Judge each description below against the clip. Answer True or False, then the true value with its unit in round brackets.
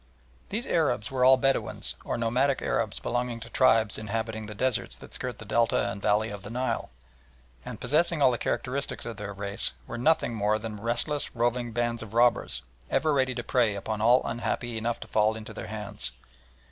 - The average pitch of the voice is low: True (115 Hz)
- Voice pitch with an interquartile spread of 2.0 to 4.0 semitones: True (2.7 semitones)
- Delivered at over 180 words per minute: True (190 wpm)